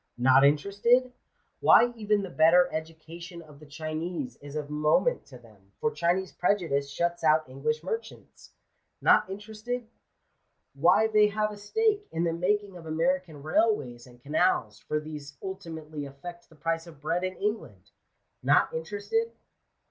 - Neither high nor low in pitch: Yes, medium, 170 Hz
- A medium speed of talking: Yes, average, 150 wpm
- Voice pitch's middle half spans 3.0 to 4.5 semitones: No, average, 5.3 semitones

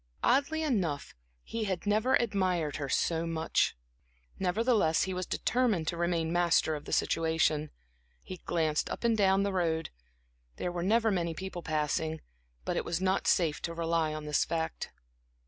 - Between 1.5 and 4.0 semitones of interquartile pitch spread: Yes, average, 3.5 semitones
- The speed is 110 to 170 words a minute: Yes, average, 165 wpm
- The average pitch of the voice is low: No, medium, 175 Hz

